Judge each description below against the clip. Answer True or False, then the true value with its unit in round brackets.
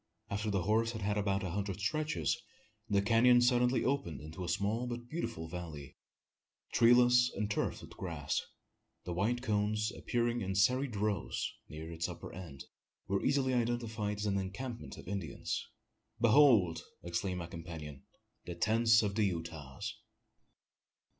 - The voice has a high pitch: False (105 Hz)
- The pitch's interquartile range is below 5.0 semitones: False (5.3 semitones)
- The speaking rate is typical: True (145 wpm)